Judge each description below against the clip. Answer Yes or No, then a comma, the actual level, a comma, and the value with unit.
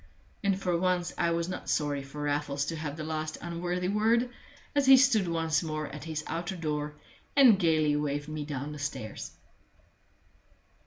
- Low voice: No, medium, 160 Hz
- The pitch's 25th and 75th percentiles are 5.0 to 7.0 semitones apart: No, average, 3.4 semitones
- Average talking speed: Yes, average, 170 wpm